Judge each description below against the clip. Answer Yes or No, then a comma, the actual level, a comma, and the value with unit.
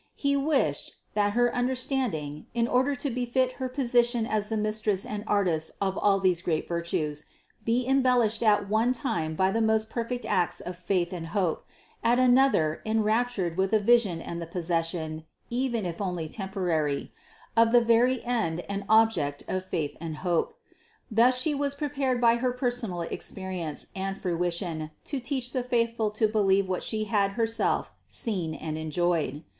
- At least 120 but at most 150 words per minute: No, average, 160 wpm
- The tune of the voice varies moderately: No, wide, 5.8 semitones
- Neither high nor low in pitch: No, high, 210 Hz